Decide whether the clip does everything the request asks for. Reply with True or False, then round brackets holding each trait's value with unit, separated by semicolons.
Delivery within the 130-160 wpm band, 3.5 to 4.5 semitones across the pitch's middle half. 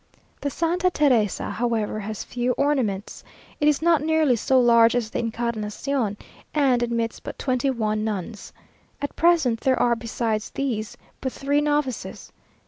True (145 wpm; 4.2 semitones)